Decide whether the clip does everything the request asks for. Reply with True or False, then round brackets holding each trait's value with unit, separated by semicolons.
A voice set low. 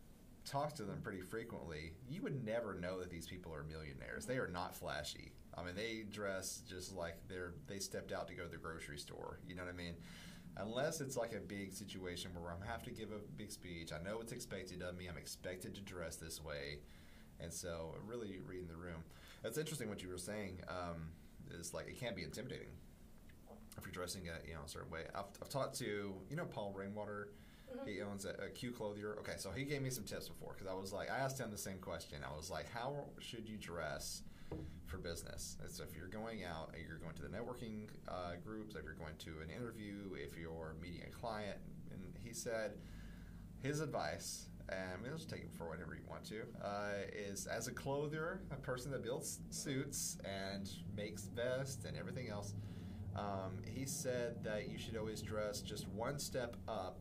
True (95 Hz)